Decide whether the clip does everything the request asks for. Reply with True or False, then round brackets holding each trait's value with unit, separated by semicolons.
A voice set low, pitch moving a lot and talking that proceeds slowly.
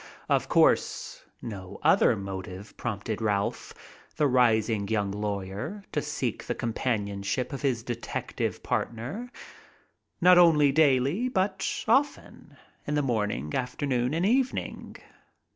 True (125 Hz; 6.7 semitones; 115 wpm)